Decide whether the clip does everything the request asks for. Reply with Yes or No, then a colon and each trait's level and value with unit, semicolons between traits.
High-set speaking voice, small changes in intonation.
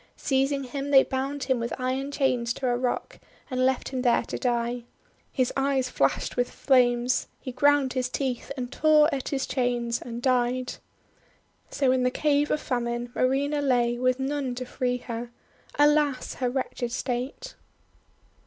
Yes: very high, 255 Hz; narrow, 2.0 semitones